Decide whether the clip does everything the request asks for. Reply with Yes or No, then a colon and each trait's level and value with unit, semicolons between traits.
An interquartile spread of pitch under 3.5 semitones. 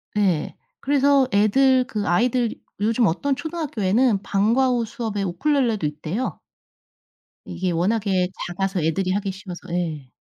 No: wide, 5.5 semitones